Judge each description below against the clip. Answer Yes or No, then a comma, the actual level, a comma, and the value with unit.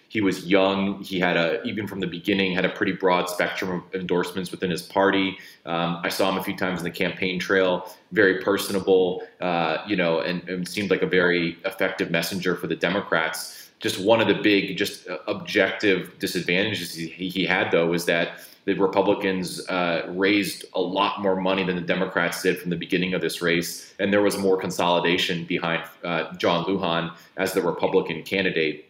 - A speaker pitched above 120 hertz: No, very low, 90 Hz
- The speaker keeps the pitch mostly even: Yes, narrow, 2.0 semitones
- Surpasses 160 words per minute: Yes, average, 190 wpm